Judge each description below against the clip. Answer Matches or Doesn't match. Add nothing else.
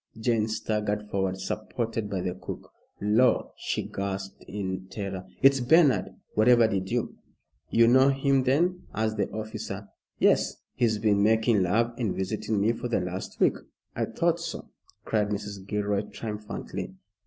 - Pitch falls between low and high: Doesn't match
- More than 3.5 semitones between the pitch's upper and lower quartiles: Doesn't match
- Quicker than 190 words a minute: Doesn't match